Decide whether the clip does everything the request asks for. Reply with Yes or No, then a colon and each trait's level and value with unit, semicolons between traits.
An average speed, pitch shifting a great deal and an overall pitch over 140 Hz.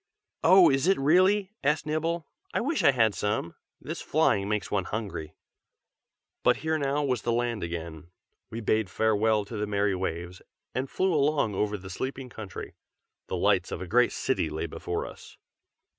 No: average, 175 wpm; wide, 6.6 semitones; low, 110 Hz